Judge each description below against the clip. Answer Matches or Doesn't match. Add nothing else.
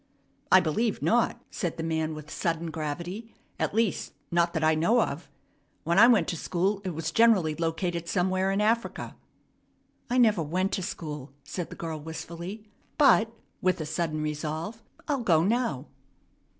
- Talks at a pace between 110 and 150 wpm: Doesn't match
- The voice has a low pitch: Doesn't match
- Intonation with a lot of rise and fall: Doesn't match